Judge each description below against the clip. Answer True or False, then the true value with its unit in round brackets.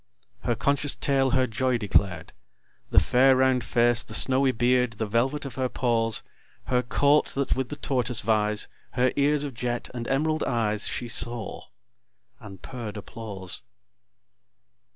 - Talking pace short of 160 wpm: True (150 wpm)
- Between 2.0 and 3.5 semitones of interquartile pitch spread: True (2.7 semitones)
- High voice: False (125 Hz)